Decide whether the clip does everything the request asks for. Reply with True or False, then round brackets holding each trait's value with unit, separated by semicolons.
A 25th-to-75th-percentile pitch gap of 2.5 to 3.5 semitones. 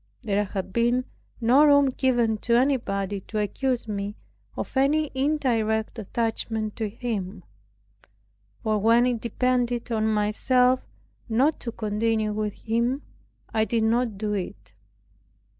True (3.0 semitones)